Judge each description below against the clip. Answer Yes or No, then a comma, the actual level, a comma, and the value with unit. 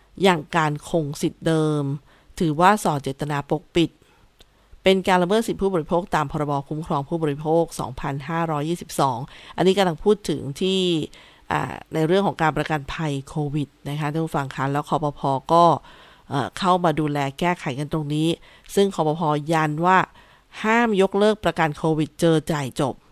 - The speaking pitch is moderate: Yes, medium, 160 Hz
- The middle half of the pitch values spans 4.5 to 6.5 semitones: No, average, 3.0 semitones